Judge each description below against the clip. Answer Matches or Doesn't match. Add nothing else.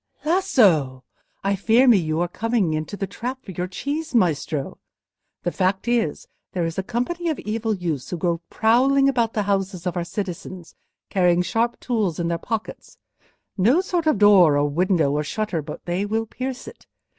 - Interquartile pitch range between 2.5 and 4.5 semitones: Doesn't match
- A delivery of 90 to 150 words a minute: Doesn't match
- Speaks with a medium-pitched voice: Doesn't match